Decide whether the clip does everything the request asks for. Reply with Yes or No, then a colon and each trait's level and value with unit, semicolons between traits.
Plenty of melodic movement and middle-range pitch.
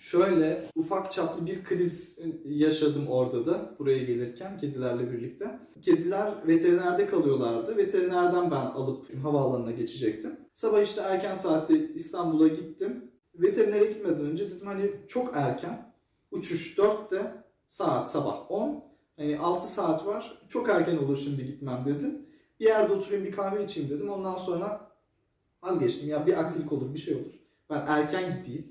Yes: wide, 5.9 semitones; medium, 175 Hz